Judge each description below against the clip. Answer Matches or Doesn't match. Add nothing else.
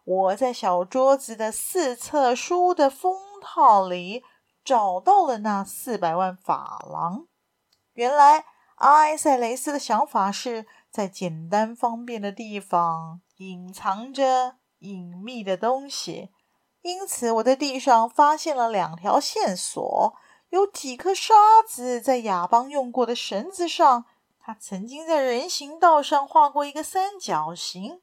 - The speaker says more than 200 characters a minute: Doesn't match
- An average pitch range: Doesn't match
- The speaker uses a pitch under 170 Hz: Doesn't match